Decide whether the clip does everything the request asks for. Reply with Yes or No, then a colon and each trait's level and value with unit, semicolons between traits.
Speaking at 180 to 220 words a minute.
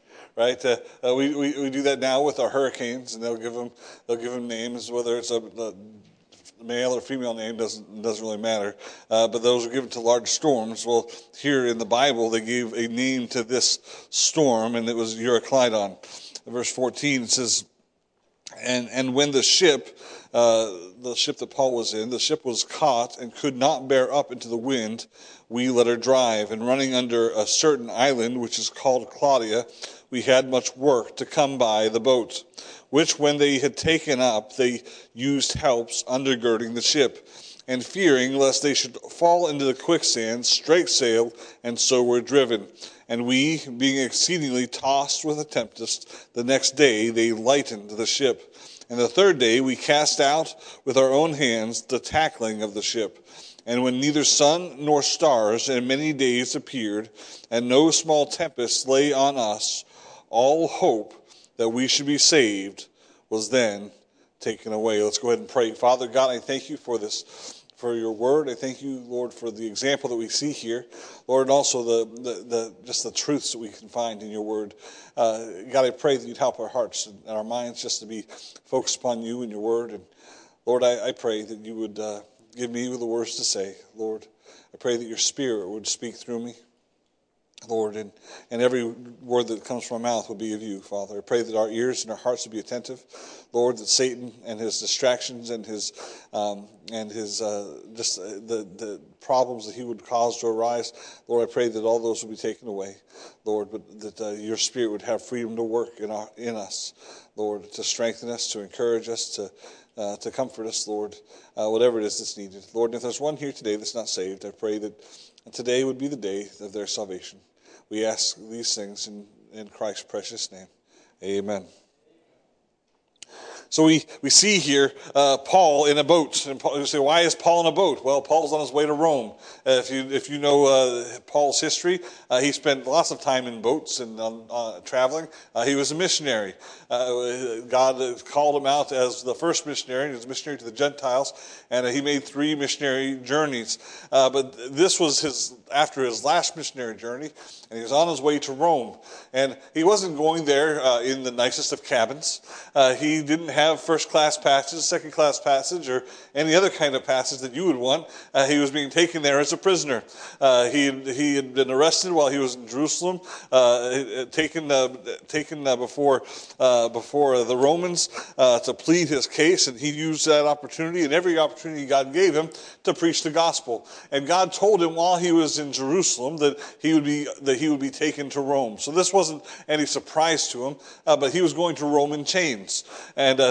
Yes: average, 200 wpm